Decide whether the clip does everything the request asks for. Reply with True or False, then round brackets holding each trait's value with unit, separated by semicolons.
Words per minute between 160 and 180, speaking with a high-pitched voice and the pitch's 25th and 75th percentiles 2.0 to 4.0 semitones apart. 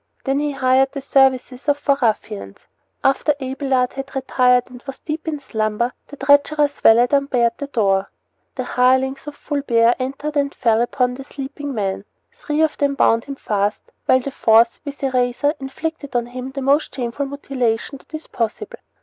True (175 wpm; 265 Hz; 2.7 semitones)